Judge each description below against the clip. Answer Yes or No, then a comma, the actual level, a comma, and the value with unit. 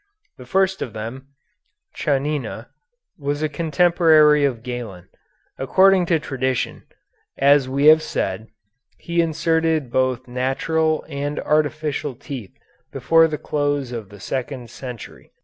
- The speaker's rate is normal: No, slow, 120 wpm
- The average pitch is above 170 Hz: No, medium, 145 Hz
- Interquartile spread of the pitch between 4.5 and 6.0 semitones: No, average, 3.6 semitones